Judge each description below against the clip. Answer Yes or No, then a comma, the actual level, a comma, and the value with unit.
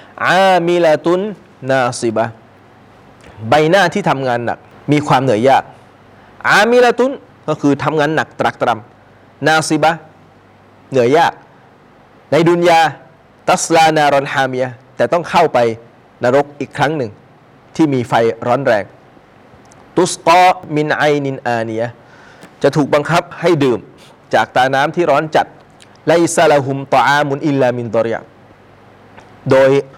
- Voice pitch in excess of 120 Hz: Yes, medium, 140 Hz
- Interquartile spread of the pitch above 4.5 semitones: Yes, average, 5.1 semitones